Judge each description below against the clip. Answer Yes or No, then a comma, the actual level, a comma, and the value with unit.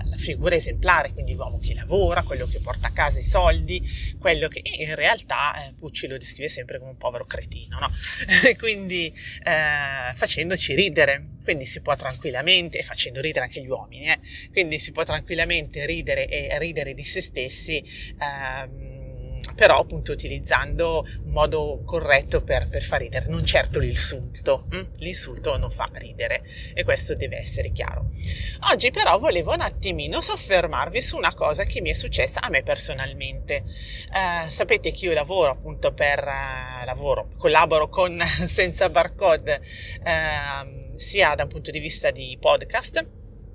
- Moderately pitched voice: Yes, medium, 155 Hz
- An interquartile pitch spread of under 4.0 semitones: No, wide, 6.5 semitones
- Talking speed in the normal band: Yes, average, 160 wpm